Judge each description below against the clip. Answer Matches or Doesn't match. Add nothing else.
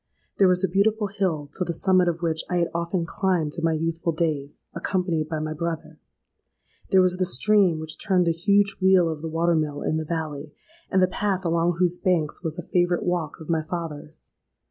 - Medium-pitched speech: Matches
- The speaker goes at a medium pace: Doesn't match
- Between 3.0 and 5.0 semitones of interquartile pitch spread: Doesn't match